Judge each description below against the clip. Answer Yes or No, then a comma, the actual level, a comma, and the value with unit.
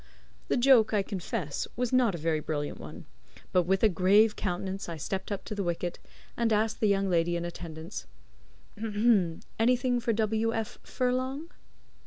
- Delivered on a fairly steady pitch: No, average, 4.8 semitones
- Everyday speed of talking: Yes, average, 165 wpm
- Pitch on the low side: No, high, 200 Hz